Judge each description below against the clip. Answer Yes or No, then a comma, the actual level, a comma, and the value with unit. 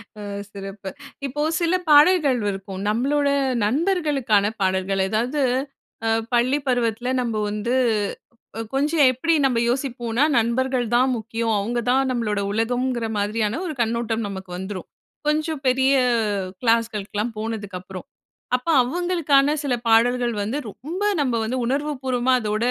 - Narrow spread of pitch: No, average, 4.1 semitones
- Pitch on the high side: Yes, high, 240 Hz